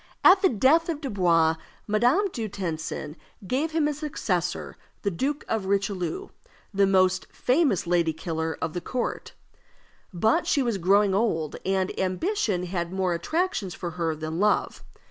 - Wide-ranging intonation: Yes, wide, 7.0 semitones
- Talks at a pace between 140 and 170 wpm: Yes, average, 150 wpm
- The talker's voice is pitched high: Yes, high, 195 Hz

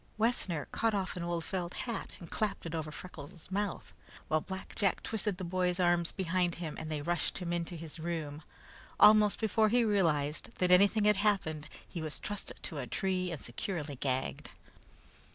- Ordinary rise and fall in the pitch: Yes, average, 4.0 semitones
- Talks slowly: No, average, 180 wpm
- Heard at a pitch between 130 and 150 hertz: No, medium, 180 Hz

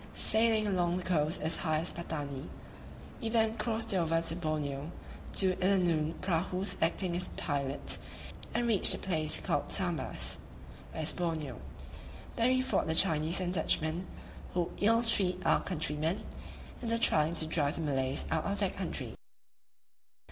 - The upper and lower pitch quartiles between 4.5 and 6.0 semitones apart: No, average, 3.8 semitones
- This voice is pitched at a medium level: Yes, medium, 170 Hz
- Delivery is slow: No, average, 150 wpm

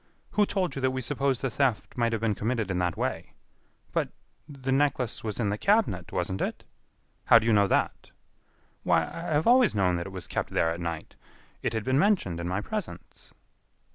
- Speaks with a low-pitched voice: Yes, low, 115 Hz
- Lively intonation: Yes, wide, 6.5 semitones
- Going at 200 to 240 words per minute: Yes, fast, 205 wpm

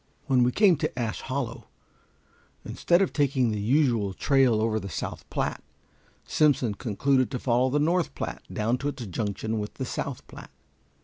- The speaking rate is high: No, average, 175 wpm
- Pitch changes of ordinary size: Yes, average, 4.3 semitones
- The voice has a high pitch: No, low, 125 Hz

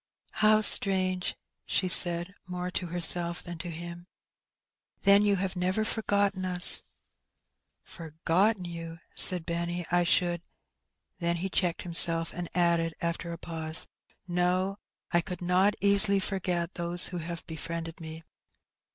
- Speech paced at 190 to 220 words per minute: No, average, 155 wpm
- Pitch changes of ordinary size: No, narrow, 1.6 semitones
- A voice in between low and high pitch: Yes, medium, 175 Hz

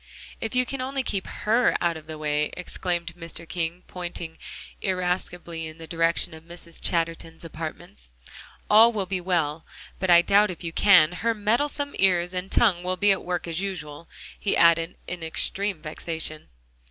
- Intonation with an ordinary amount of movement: Yes, average, 3.0 semitones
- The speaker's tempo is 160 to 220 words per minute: Yes, average, 170 wpm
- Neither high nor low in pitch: Yes, medium, 175 Hz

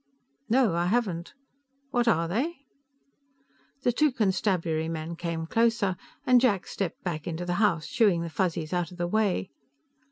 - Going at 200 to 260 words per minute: No, average, 155 wpm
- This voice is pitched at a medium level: Yes, medium, 180 Hz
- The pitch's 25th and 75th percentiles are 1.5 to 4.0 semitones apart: No, average, 5.1 semitones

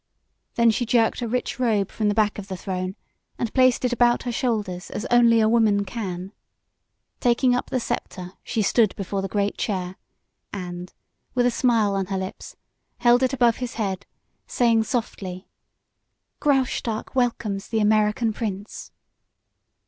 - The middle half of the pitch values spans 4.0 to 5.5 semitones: No, average, 3.6 semitones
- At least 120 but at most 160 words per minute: Yes, average, 155 wpm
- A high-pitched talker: Yes, high, 220 Hz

